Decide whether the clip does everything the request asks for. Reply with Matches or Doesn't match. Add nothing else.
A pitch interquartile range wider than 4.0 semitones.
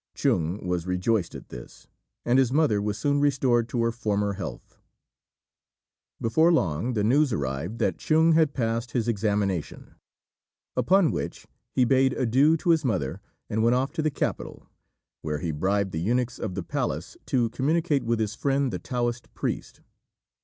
Matches